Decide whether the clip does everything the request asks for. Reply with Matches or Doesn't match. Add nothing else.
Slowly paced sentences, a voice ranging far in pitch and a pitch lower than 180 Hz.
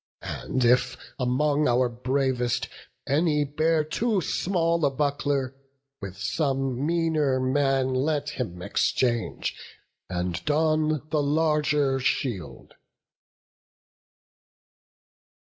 Doesn't match